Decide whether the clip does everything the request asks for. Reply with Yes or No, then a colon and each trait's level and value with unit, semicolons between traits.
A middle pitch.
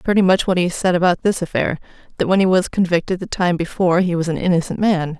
Yes: medium, 175 Hz